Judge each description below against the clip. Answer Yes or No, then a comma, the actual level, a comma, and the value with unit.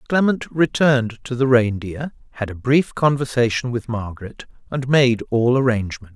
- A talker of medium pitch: No, low, 125 Hz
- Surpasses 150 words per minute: No, average, 145 wpm